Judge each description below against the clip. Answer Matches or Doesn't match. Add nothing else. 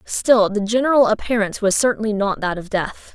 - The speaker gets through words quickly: Doesn't match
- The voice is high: Matches